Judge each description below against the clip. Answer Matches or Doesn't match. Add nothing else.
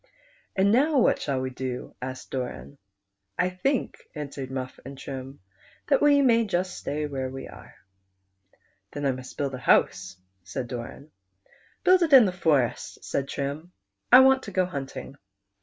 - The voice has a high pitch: Doesn't match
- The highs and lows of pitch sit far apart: Matches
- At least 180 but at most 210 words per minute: Matches